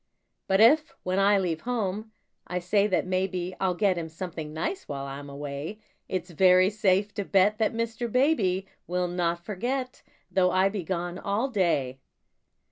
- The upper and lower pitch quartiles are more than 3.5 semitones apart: No, average, 3.2 semitones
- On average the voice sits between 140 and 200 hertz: Yes, medium, 185 Hz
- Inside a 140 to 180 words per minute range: Yes, average, 165 wpm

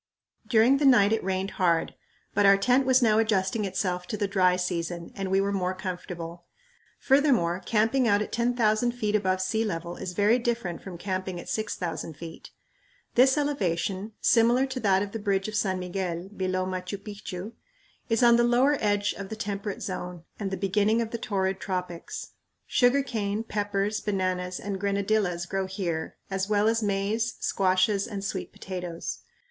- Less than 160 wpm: No, average, 175 wpm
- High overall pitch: Yes, high, 200 Hz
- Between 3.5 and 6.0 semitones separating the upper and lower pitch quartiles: No, average, 3.1 semitones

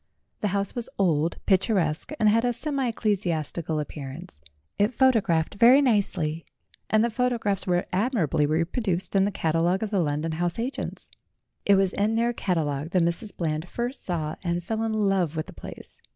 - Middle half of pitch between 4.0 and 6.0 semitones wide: Yes, average, 5.3 semitones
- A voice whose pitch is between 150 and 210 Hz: Yes, high, 190 Hz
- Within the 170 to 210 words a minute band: Yes, average, 180 wpm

